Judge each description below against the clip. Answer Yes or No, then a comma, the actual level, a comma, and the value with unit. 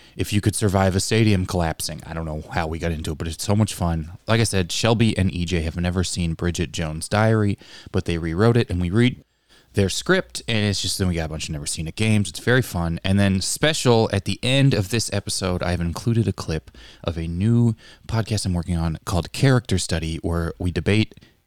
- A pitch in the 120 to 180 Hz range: No, very low, 95 Hz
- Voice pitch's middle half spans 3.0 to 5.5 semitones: Yes, average, 4.4 semitones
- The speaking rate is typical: No, fast, 230 wpm